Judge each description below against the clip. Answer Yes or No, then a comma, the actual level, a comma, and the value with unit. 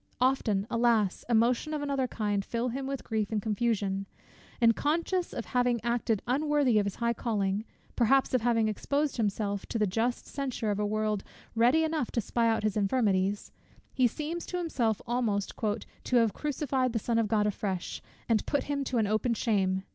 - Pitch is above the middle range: Yes, high, 230 Hz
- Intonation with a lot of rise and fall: No, average, 3.5 semitones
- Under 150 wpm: No, average, 185 wpm